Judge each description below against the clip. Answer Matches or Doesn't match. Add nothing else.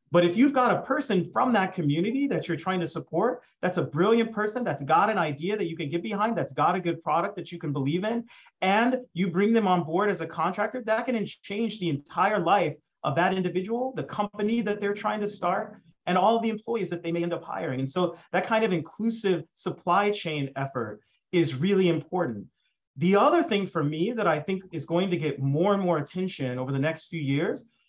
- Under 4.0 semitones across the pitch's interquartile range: Doesn't match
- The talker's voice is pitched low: Doesn't match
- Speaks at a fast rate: Matches